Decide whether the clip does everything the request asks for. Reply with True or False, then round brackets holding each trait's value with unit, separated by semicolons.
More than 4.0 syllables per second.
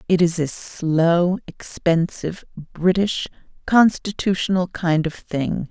False (3.8 syllables/s)